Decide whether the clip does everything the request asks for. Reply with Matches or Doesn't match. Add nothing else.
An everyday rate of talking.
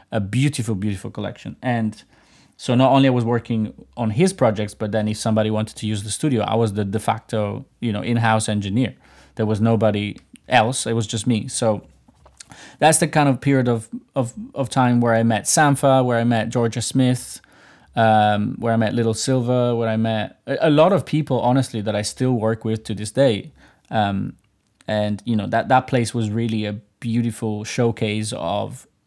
Matches